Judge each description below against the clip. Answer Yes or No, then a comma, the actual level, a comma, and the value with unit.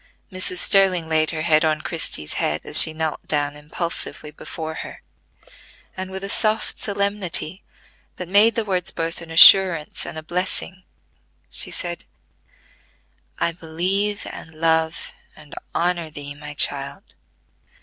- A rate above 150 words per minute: No, average, 140 wpm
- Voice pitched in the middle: Yes, medium, 165 Hz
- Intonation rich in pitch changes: No, average, 3.2 semitones